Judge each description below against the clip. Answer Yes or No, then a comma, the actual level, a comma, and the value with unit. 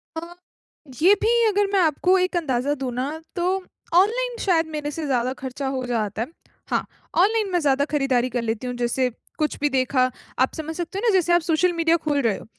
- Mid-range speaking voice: No, very high, 300 Hz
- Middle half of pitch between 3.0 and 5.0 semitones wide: No, wide, 5.5 semitones